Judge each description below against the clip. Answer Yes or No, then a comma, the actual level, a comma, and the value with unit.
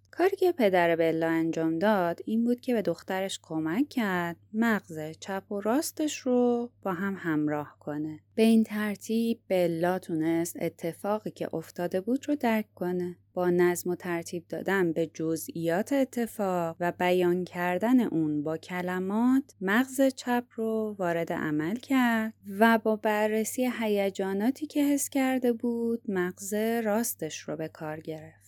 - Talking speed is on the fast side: No, average, 145 wpm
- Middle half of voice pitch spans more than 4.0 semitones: Yes, average, 5.3 semitones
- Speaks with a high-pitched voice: Yes, high, 195 Hz